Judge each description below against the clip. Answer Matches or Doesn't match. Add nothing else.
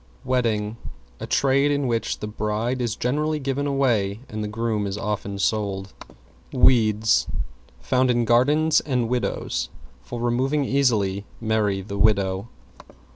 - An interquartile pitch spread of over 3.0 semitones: Matches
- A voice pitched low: Matches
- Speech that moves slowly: Matches